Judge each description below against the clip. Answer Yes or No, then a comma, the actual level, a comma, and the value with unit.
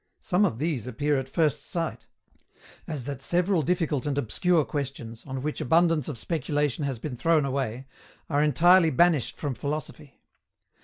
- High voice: No, medium, 145 Hz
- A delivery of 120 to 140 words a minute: No, average, 155 wpm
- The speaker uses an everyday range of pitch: Yes, average, 3.7 semitones